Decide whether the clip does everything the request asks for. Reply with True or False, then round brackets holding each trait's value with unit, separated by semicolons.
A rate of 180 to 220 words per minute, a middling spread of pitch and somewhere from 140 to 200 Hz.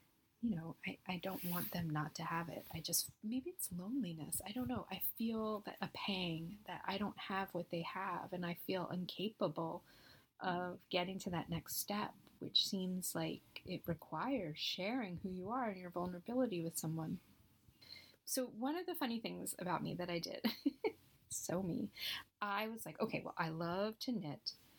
True (185 wpm; 4.5 semitones; 185 Hz)